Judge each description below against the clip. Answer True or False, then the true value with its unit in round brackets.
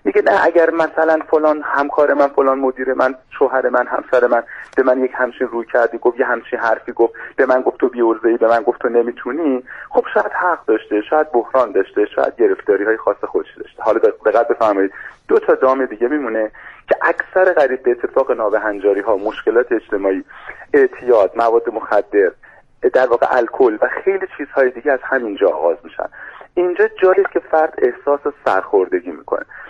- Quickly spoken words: True (180 wpm)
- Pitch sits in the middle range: True (160 Hz)